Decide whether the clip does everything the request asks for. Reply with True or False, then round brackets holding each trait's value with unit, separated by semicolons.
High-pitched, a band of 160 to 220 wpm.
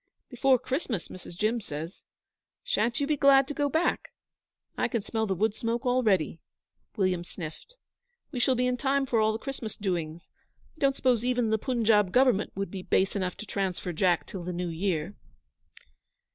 True (220 Hz; 180 wpm)